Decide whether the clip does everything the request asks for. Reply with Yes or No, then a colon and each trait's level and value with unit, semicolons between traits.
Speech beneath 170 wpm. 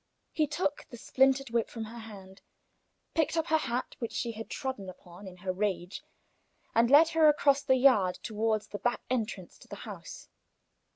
No: average, 180 wpm